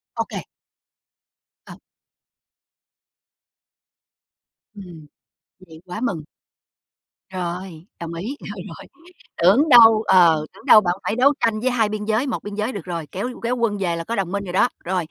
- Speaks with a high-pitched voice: Yes, high, 200 Hz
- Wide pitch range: No, average, 4.4 semitones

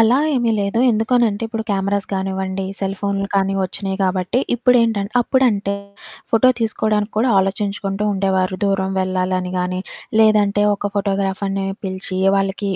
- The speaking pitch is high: Yes, high, 200 Hz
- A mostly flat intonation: Yes, narrow, 2.0 semitones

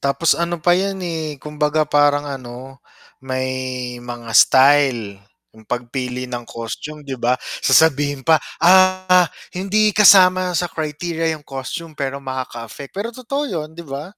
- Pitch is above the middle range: No, medium, 145 Hz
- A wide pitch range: No, average, 4.8 semitones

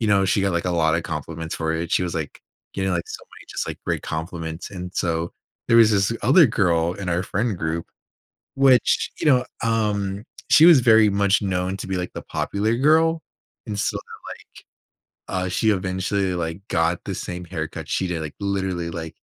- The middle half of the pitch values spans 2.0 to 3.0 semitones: No, average, 3.9 semitones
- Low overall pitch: Yes, very low, 95 Hz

